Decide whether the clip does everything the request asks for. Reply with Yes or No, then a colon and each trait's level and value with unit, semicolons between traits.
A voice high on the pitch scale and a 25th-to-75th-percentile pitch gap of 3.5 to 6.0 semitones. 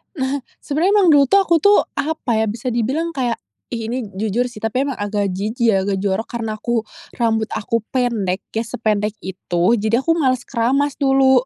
Yes: high, 235 Hz; average, 4.0 semitones